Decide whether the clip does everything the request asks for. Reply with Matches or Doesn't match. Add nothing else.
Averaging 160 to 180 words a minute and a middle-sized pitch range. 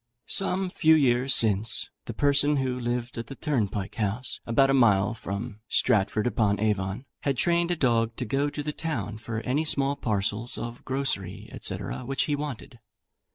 Matches